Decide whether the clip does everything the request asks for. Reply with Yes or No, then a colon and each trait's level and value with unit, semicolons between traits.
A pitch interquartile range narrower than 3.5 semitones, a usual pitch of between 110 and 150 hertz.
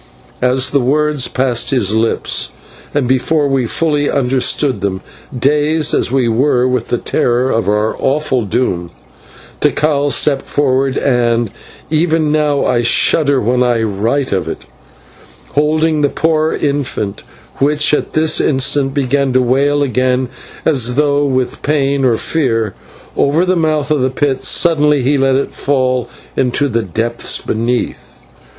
Yes: average, 3.1 semitones; low, 135 Hz